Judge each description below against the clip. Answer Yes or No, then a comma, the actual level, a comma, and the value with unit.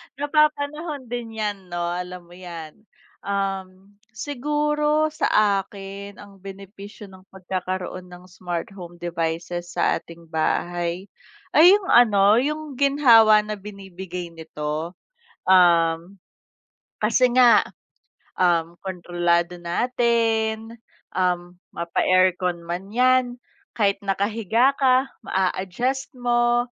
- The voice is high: Yes, high, 195 Hz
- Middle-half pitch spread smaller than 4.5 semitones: No, average, 5.3 semitones